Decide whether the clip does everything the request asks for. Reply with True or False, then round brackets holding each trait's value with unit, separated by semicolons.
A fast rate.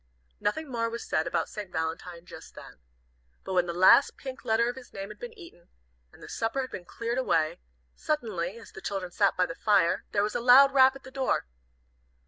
True (215 wpm)